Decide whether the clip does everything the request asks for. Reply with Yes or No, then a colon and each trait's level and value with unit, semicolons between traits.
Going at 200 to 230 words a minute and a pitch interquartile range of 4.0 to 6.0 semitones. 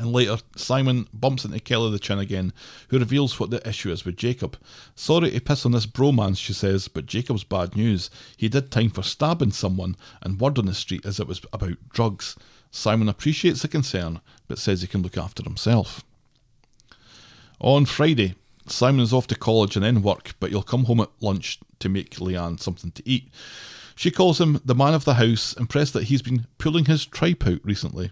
Yes: fast, 205 wpm; average, 4.7 semitones